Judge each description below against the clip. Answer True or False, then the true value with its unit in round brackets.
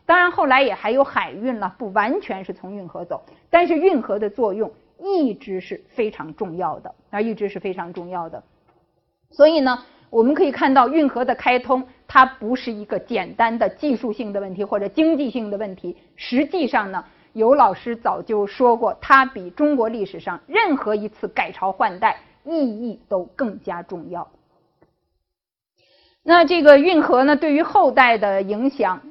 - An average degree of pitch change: False (6.0 semitones)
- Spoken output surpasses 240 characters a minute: True (255 characters per minute)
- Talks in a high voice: True (235 Hz)